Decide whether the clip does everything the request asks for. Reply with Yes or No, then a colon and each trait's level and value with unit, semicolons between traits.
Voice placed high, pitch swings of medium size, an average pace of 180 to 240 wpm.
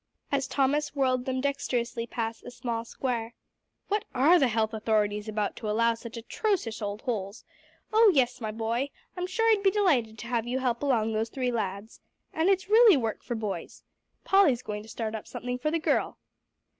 Yes: high, 240 Hz; average, 4.2 semitones; average, 190 wpm